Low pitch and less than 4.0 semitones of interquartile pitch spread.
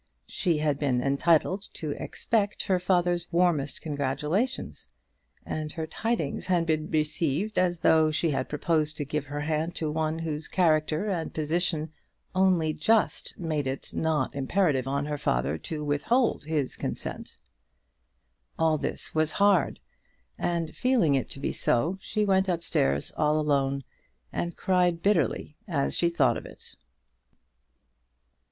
No: medium, 160 Hz; average, 3.1 semitones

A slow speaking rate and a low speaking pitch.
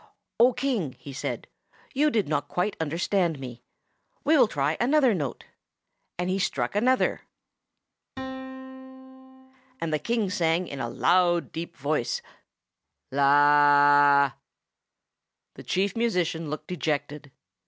No: slow, 110 wpm; medium, 180 Hz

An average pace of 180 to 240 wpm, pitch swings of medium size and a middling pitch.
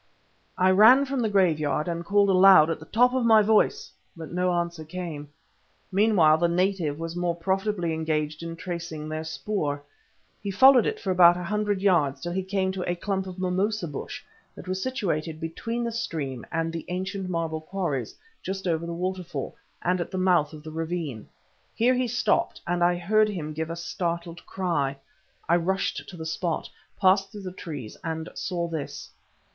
Yes: average, 185 wpm; average, 3.2 semitones; medium, 175 Hz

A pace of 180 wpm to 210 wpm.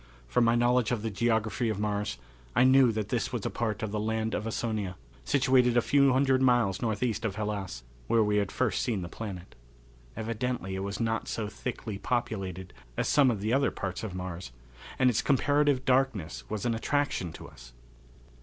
Yes: average, 190 wpm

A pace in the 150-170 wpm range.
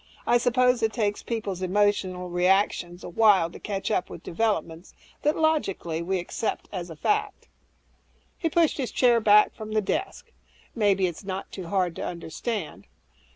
Yes: average, 165 wpm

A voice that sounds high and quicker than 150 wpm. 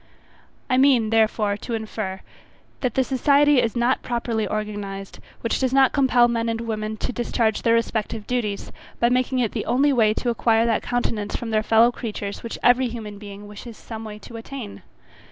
Yes: high, 230 Hz; average, 185 wpm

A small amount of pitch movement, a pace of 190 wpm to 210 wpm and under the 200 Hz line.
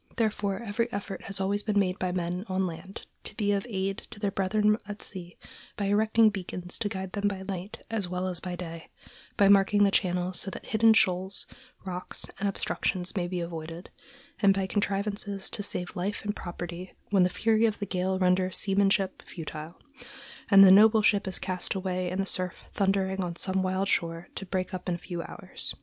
Yes: narrow, 2.0 semitones; average, 200 wpm; high, 190 Hz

